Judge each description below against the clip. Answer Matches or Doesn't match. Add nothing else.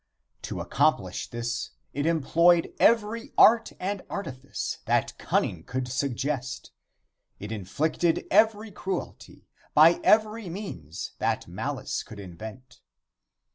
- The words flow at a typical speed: Doesn't match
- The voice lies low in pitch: Doesn't match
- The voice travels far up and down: Matches